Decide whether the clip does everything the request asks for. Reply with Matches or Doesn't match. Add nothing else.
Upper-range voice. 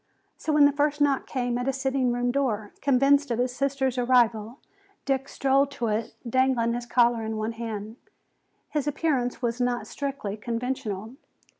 Matches